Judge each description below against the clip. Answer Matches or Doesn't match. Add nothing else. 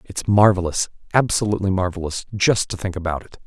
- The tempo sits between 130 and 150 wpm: Matches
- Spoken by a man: Matches